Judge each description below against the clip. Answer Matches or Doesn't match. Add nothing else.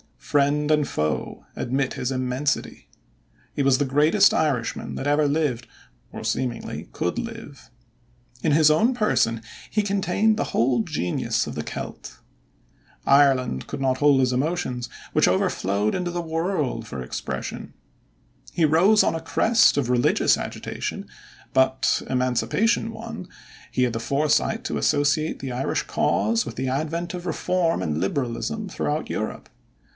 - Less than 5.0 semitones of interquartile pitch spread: Doesn't match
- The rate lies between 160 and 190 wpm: Doesn't match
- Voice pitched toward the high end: Doesn't match